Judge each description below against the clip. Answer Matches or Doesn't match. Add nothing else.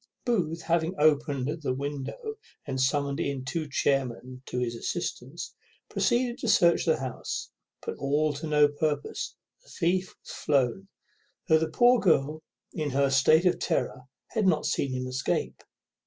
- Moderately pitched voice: Matches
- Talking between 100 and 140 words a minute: Doesn't match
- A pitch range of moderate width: Matches